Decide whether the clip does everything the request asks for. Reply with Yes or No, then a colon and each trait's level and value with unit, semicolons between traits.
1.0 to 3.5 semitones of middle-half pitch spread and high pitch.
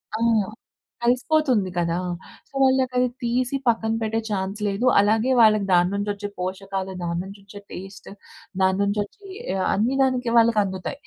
No: average, 4.1 semitones; high, 210 Hz